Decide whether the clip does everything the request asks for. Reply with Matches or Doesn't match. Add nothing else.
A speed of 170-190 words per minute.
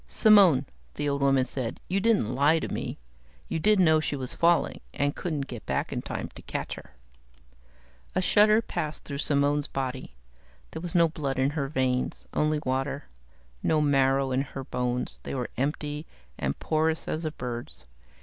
Matches